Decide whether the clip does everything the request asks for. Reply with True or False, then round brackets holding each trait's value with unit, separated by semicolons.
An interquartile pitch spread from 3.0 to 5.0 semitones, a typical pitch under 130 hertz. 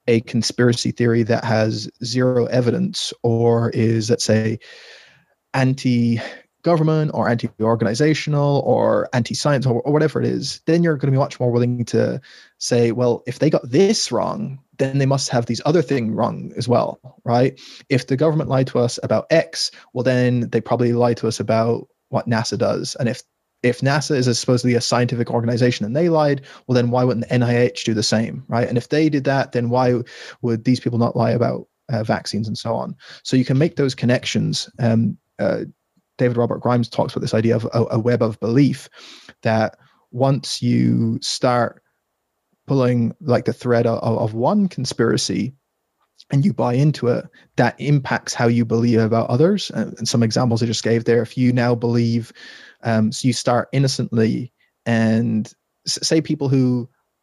False (2.4 semitones; 120 Hz)